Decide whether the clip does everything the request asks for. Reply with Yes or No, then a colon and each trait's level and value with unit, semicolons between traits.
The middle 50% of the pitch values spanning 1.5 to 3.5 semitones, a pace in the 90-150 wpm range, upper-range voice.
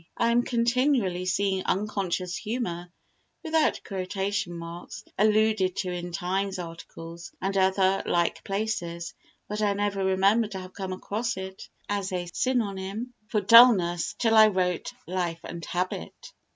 Yes: average, 3.0 semitones; average, 140 wpm; high, 195 Hz